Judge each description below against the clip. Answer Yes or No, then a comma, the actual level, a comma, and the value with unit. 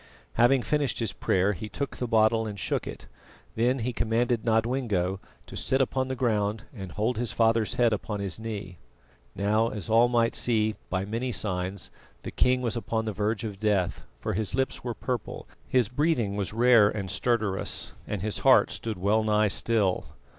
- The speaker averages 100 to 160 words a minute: No, average, 180 wpm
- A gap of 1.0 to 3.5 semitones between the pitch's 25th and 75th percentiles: Yes, average, 2.9 semitones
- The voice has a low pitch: Yes, low, 110 Hz